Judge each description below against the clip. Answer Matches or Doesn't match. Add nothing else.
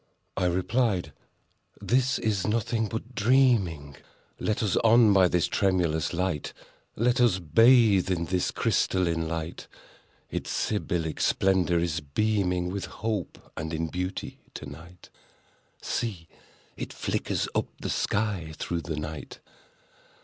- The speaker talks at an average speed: Doesn't match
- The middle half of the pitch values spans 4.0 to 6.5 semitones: Matches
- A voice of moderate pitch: Doesn't match